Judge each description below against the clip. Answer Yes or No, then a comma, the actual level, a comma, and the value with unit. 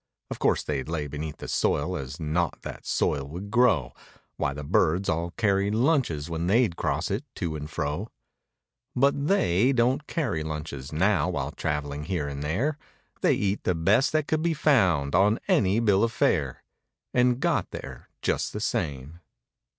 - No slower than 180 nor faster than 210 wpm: No, average, 170 wpm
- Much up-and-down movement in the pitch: Yes, wide, 7.7 semitones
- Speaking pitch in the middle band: No, very low, 90 Hz